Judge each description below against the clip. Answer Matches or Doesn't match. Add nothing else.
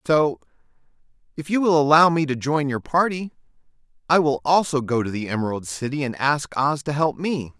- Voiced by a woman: Doesn't match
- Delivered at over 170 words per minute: Matches